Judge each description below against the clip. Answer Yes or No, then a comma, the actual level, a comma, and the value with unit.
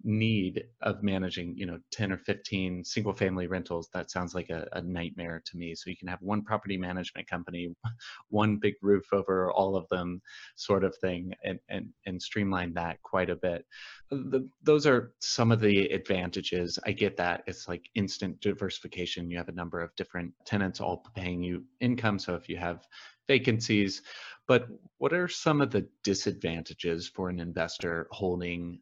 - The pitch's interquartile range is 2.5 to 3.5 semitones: Yes, average, 2.8 semitones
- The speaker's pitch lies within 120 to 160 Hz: No, very low, 95 Hz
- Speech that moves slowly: No, average, 180 wpm